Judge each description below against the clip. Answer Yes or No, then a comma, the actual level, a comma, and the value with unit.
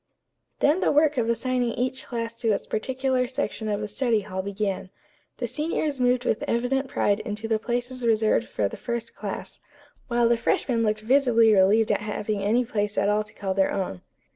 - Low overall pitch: No, high, 230 Hz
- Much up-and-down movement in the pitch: No, average, 3.1 semitones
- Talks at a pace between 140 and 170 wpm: No, average, 190 wpm